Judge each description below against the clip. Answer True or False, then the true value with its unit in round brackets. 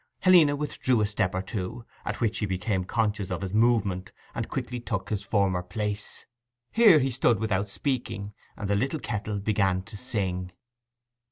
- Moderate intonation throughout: True (3.9 semitones)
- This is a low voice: True (105 Hz)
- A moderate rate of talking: True (170 wpm)